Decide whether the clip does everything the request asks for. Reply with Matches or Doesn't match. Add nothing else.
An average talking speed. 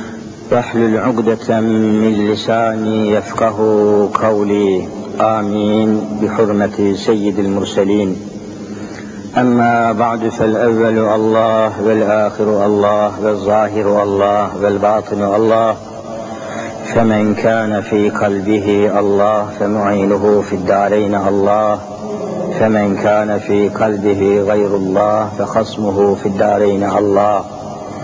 Doesn't match